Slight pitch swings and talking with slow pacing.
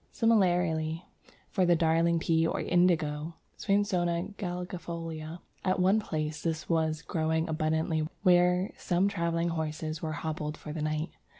Yes: narrow, 2.2 semitones; slow, 130 wpm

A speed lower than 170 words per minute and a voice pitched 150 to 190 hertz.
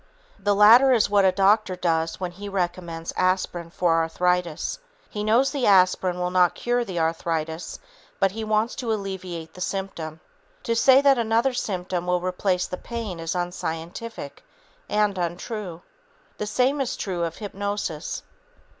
Yes: average, 155 wpm; medium, 185 Hz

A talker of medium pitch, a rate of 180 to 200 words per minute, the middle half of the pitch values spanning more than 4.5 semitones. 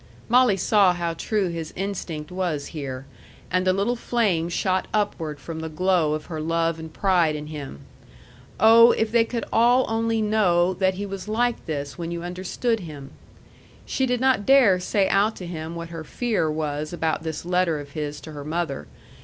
Yes: medium, 175 Hz; average, 185 wpm; average, 4.9 semitones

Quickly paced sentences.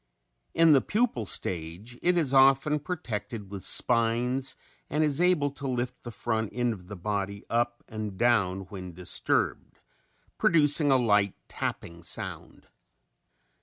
No: slow, 135 wpm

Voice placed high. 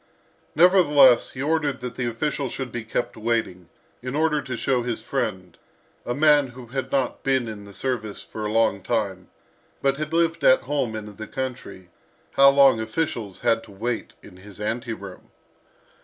No: low, 120 Hz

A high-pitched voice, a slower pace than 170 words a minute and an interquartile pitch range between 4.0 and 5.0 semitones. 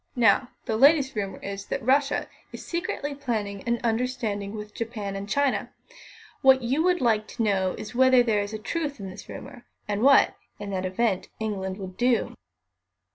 No: high, 225 Hz; average, 175 wpm; average, 4.4 semitones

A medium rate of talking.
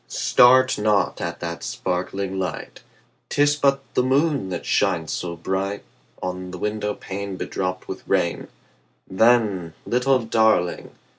No: slow, 130 wpm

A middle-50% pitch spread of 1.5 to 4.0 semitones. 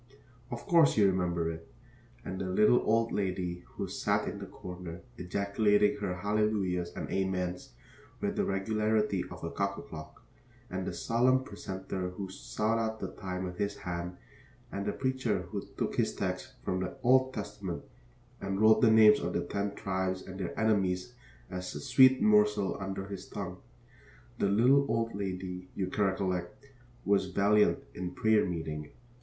Yes: average, 2.8 semitones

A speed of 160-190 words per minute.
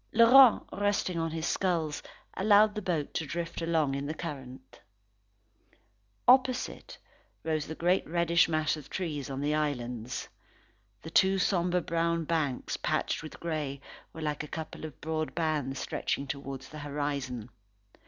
No: average, 145 wpm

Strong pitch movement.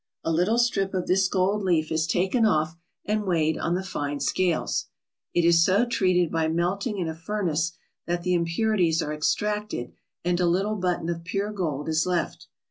No: average, 3.2 semitones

